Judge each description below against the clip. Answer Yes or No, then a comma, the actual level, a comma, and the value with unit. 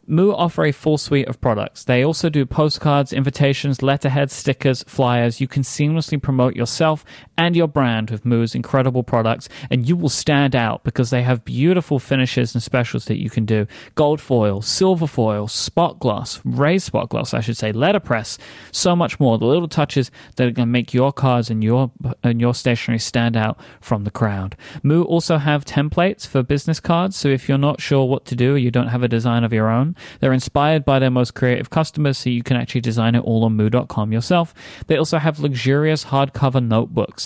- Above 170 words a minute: Yes, average, 200 wpm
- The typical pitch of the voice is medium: No, low, 130 Hz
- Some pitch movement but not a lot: Yes, average, 3.8 semitones